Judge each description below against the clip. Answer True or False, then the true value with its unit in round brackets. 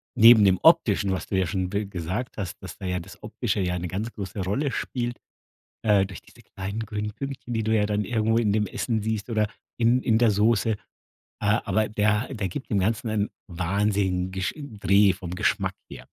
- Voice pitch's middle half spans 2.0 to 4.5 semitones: True (2.7 semitones)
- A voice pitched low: True (105 Hz)